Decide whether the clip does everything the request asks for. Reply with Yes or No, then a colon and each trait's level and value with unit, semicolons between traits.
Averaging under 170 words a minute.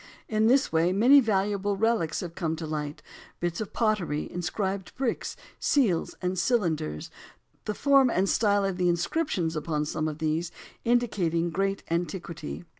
Yes: average, 150 wpm